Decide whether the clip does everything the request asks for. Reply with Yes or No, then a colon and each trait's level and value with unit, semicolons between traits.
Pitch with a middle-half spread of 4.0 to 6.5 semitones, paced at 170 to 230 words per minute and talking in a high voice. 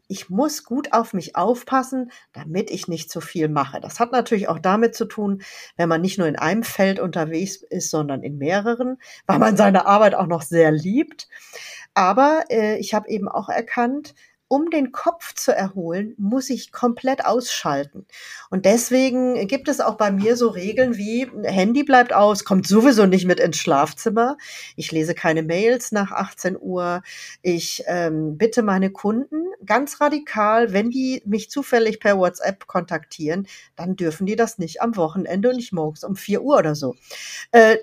Yes: wide, 5.4 semitones; average, 175 wpm; high, 210 Hz